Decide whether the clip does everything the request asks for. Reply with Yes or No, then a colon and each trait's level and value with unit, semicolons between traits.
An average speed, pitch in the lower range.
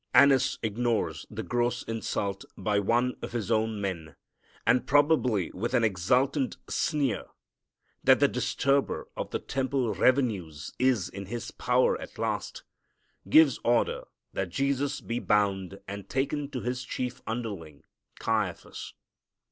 No: slow, 130 wpm; low, 120 Hz